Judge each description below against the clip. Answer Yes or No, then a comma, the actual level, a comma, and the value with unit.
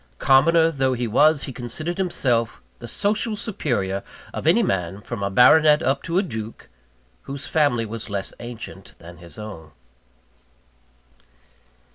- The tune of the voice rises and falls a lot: Yes, wide, 6.6 semitones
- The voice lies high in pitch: No, low, 125 Hz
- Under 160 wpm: Yes, average, 140 wpm